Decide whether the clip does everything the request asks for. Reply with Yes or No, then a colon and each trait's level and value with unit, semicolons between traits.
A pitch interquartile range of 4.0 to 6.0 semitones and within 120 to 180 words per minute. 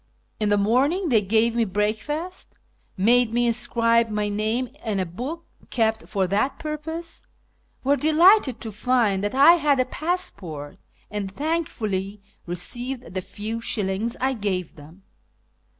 Yes: average, 5.1 semitones; average, 145 wpm